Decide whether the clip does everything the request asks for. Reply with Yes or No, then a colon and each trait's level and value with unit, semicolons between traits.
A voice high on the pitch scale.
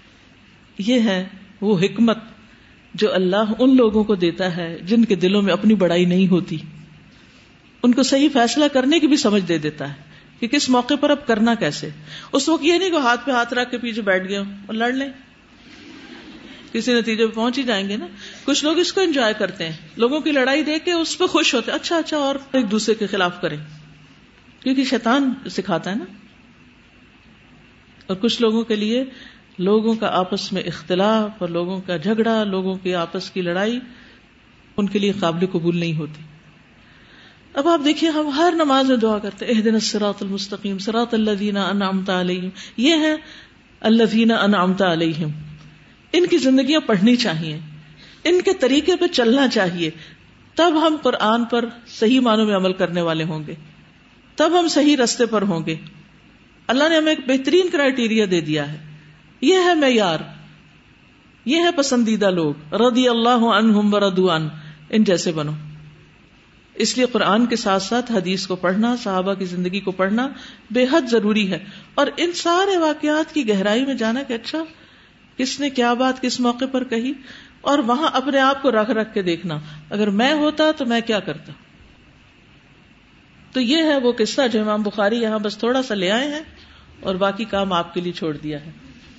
Yes: high, 220 Hz